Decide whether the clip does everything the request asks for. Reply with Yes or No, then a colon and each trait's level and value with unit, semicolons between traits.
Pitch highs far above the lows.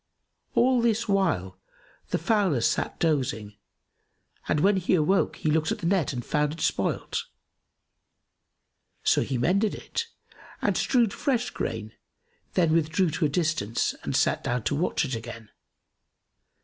Yes: wide, 7.6 semitones